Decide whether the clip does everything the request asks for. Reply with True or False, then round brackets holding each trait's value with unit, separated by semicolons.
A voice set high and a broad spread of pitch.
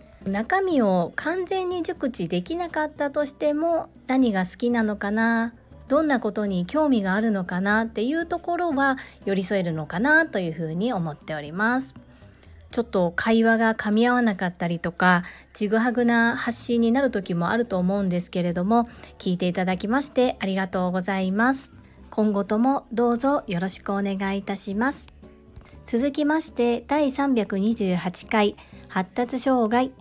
True (225 Hz; 5.7 semitones)